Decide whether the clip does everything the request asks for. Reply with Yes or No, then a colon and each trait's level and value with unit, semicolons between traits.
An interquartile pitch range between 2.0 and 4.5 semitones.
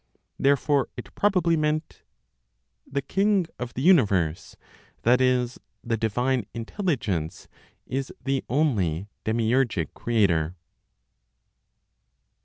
No: average, 5.1 semitones